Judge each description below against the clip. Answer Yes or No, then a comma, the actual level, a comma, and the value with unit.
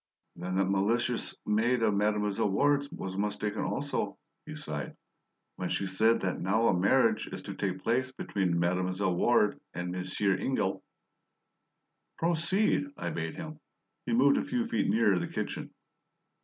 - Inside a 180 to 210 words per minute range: No, average, 155 wpm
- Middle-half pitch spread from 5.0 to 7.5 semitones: Yes, wide, 5.5 semitones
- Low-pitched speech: Yes, low, 105 Hz